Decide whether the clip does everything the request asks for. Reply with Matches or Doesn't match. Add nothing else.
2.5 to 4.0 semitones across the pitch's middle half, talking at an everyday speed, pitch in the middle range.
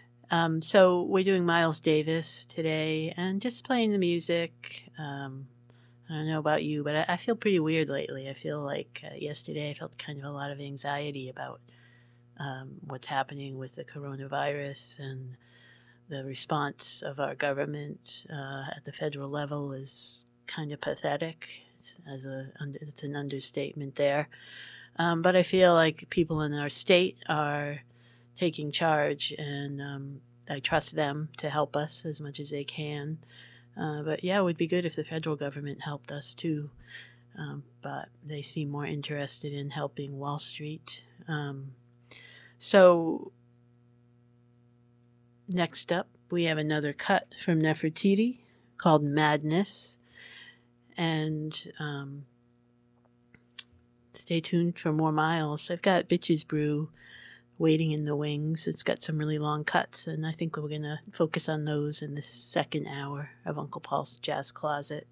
Matches